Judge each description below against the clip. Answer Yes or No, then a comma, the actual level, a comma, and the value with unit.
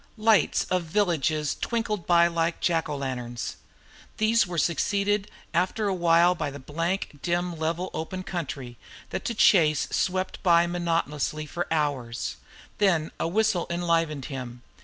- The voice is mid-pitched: Yes, medium, 170 Hz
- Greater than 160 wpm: No, average, 145 wpm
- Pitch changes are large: No, average, 3.4 semitones